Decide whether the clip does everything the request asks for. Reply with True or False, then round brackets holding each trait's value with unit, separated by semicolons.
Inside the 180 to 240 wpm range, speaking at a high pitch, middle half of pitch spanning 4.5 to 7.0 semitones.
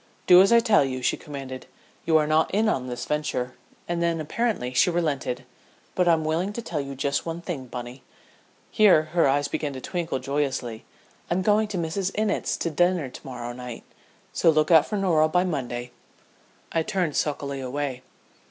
False (185 wpm; 155 Hz; 5.0 semitones)